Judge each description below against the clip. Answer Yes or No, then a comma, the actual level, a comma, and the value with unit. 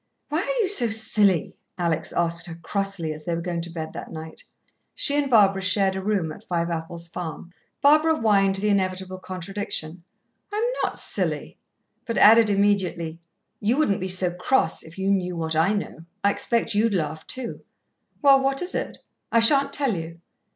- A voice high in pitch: Yes, high, 195 Hz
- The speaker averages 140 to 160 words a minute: No, average, 180 wpm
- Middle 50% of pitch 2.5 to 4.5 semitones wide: No, average, 5.0 semitones